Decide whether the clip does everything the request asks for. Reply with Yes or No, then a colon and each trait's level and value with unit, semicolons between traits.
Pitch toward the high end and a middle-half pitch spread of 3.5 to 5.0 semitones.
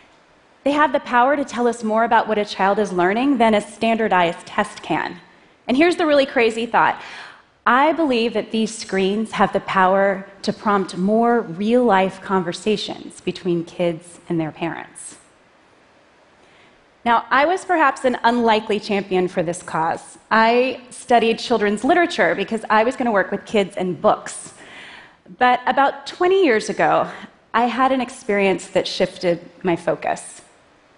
Yes: high, 215 Hz; average, 4.2 semitones